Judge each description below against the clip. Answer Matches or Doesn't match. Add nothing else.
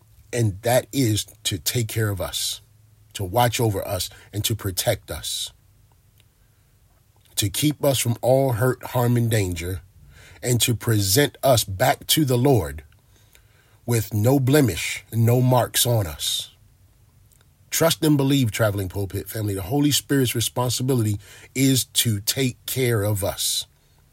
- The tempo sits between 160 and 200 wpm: Doesn't match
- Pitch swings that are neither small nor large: Matches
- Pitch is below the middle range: Matches